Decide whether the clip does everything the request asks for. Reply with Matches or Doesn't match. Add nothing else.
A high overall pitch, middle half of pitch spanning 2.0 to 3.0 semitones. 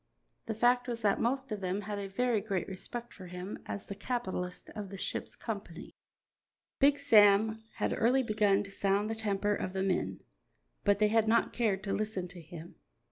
Matches